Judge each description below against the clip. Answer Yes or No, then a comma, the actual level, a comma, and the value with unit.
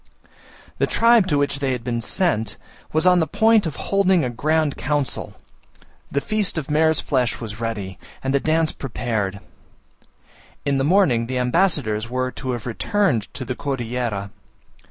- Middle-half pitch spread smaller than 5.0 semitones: No, average, 5.3 semitones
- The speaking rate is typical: Yes, average, 160 wpm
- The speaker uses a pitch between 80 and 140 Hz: Yes, low, 135 Hz